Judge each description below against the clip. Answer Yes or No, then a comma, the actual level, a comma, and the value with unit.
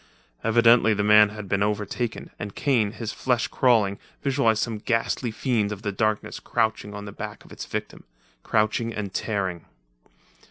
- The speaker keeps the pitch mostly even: Yes, narrow, 2.1 semitones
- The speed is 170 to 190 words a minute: No, average, 160 wpm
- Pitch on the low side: Yes, low, 110 Hz